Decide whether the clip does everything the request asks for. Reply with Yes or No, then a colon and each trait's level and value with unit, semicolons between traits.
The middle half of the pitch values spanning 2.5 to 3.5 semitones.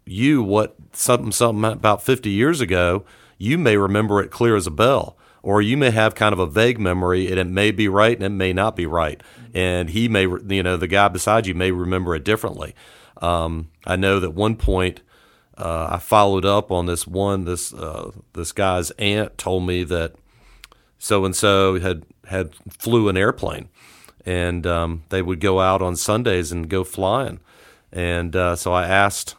Yes: average, 2.8 semitones